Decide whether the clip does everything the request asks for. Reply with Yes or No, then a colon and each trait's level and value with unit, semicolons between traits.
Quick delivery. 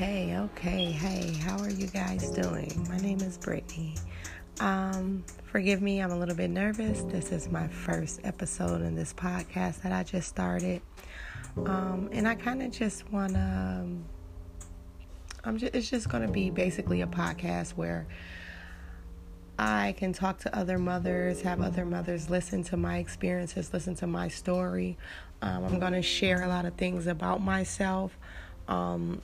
No: average, 155 wpm